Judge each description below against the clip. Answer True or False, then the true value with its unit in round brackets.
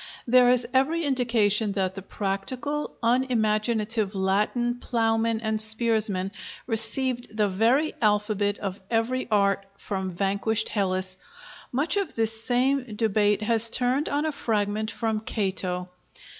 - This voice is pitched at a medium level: False (220 Hz)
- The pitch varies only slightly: False (3.2 semitones)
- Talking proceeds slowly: True (125 wpm)